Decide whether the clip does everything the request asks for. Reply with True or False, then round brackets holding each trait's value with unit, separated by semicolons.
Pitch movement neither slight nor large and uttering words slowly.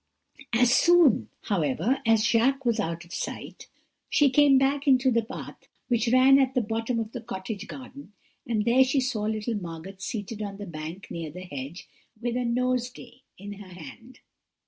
False (4.5 semitones; 175 wpm)